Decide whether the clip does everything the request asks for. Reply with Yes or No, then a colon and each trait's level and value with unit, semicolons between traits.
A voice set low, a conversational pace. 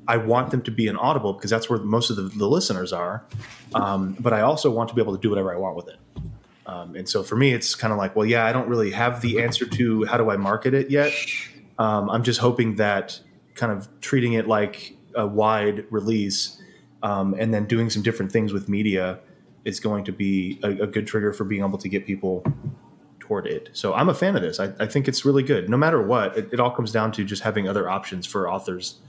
No: low, 110 Hz; fast, 250 wpm